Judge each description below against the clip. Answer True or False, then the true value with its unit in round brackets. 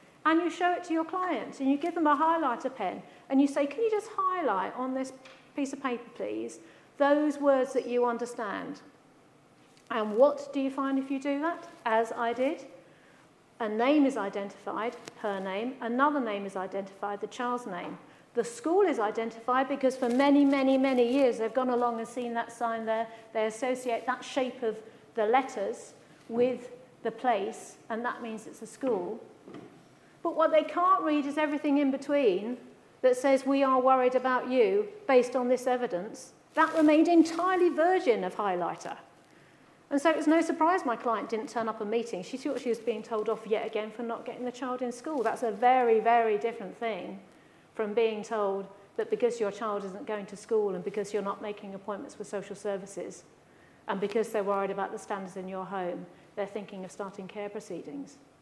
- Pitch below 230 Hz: False (245 Hz)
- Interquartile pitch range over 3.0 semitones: True (4.3 semitones)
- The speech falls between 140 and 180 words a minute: False (195 wpm)